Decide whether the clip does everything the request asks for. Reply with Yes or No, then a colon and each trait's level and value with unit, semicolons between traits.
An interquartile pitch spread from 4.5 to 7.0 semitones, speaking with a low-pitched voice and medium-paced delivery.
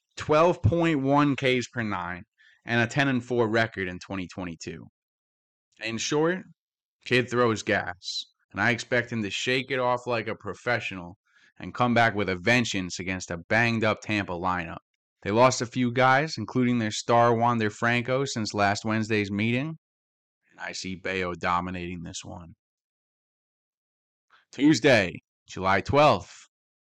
Yes: average, 4.8 semitones; low, 110 Hz; average, 150 wpm